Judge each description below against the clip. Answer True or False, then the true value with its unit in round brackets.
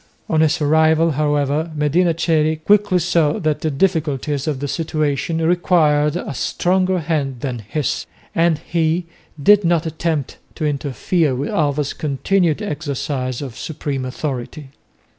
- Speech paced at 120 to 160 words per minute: True (135 wpm)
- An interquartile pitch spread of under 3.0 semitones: True (2.6 semitones)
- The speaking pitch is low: False (155 Hz)